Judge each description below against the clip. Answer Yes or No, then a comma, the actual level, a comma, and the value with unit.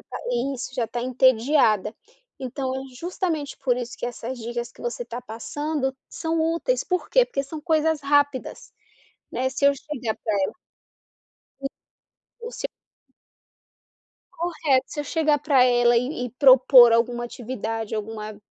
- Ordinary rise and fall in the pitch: Yes, average, 3.7 semitones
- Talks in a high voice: Yes, very high, 260 Hz